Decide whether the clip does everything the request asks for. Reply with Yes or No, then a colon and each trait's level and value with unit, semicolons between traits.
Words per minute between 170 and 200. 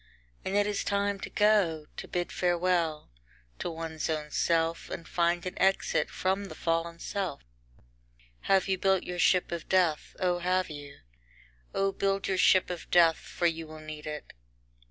Yes: average, 175 wpm